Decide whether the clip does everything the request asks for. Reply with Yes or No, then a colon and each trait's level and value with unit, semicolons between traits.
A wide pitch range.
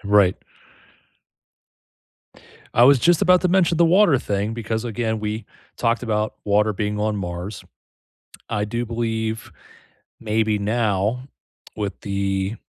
No: narrow, 2.5 semitones